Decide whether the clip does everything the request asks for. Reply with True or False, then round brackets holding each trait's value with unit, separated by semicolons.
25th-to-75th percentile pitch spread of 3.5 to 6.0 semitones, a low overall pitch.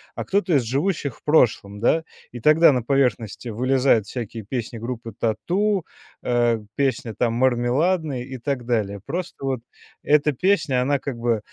True (4.1 semitones; 125 Hz)